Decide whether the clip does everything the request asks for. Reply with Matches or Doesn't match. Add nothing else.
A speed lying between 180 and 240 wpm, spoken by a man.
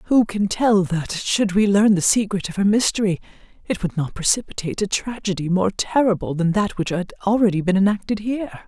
Doesn't match